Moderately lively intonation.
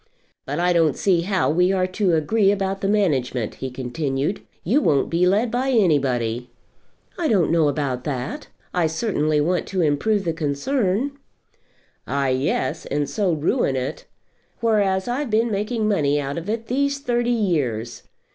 No: wide, 6.9 semitones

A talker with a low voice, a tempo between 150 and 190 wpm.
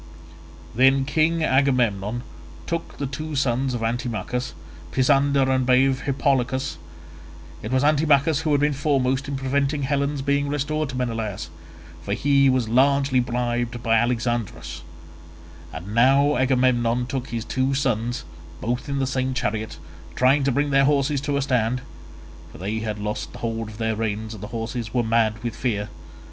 Yes: low, 130 Hz; average, 155 wpm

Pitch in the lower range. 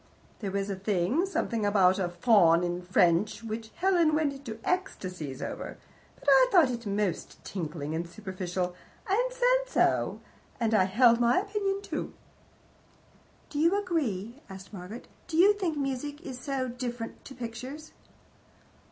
No: high, 235 Hz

